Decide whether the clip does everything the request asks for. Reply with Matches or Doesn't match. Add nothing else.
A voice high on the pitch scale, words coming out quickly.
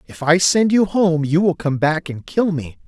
Doesn't match